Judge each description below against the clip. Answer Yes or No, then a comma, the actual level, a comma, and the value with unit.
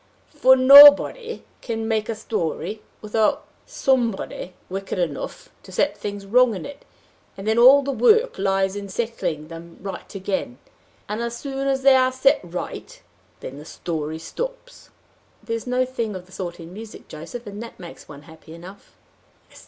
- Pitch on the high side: Yes, high, 215 Hz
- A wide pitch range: Yes, wide, 6.1 semitones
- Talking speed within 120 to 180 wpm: Yes, average, 165 wpm